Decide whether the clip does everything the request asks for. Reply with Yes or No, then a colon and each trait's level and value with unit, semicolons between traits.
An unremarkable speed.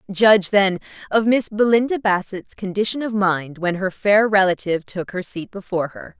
Yes: average, 175 wpm